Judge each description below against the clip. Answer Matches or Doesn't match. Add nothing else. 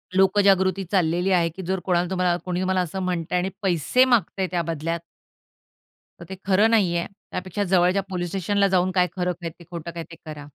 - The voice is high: Doesn't match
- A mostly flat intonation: Matches